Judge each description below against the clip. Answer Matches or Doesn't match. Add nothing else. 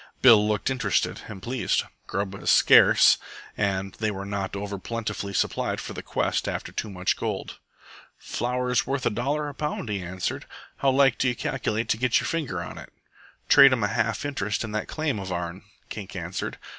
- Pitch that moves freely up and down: Doesn't match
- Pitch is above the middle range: Doesn't match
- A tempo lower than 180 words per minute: Doesn't match